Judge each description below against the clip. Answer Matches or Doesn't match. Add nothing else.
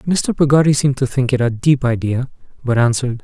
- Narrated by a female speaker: Doesn't match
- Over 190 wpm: Matches